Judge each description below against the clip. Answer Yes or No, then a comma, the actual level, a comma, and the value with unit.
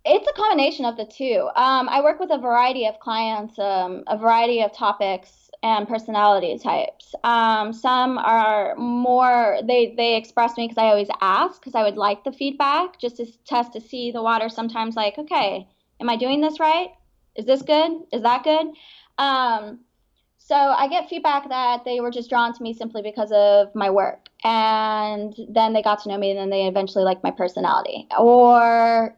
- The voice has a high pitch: Yes, high, 235 Hz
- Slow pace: No, average, 190 wpm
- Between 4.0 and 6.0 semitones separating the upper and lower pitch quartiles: No, average, 3.3 semitones